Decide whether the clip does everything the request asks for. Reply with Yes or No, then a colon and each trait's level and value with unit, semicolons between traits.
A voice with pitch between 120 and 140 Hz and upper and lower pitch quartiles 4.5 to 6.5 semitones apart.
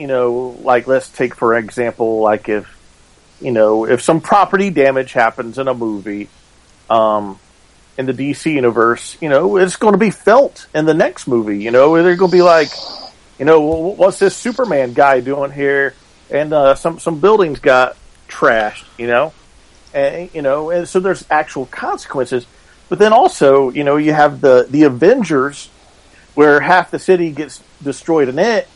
Yes: low, 135 Hz; wide, 5.5 semitones